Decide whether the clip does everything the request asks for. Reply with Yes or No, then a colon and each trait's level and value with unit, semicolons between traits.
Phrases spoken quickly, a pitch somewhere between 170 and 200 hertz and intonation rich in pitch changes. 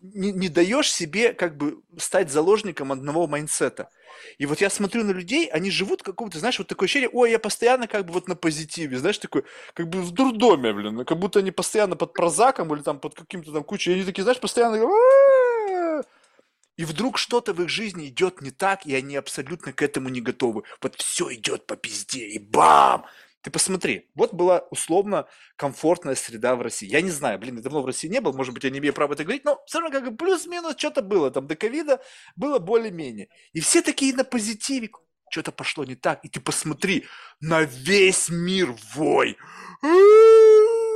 Yes: fast, 195 wpm; medium, 185 Hz; wide, 8.4 semitones